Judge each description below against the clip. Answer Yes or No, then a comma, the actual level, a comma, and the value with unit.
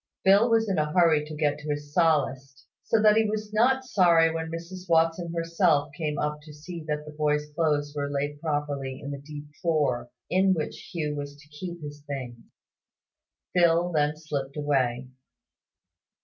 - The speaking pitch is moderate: Yes, medium, 150 Hz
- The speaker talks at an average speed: Yes, average, 175 wpm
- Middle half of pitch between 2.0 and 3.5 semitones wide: Yes, average, 2.7 semitones